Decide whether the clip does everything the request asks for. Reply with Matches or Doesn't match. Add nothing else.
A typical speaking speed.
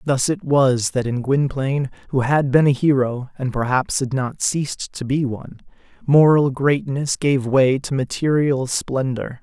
Matches